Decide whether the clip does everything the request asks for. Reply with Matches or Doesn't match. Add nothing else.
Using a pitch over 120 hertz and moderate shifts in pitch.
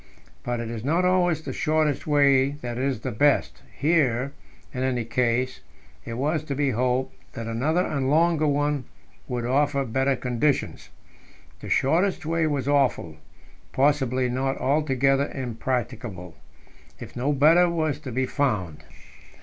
Matches